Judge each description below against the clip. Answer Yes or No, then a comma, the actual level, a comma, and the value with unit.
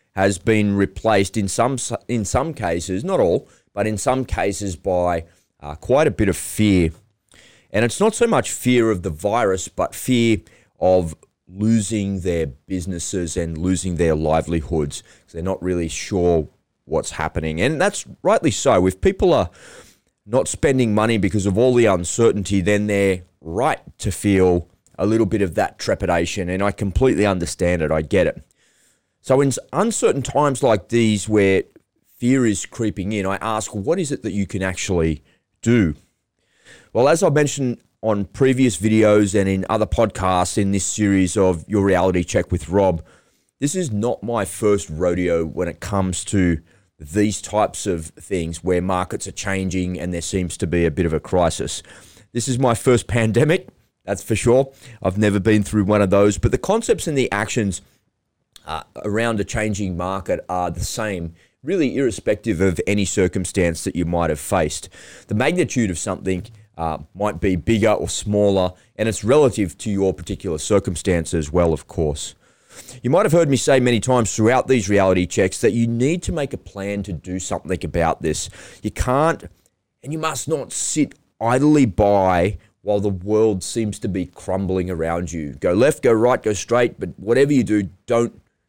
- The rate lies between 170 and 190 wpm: Yes, average, 180 wpm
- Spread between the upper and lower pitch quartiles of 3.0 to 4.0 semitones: Yes, average, 3.7 semitones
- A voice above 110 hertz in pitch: No, low, 100 Hz